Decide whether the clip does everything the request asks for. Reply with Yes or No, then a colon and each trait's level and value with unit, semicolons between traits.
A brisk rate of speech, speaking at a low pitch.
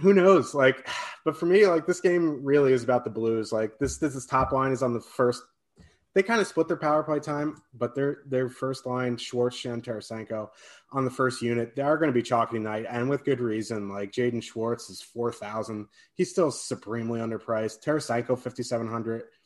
Yes: fast, 215 wpm; low, 125 Hz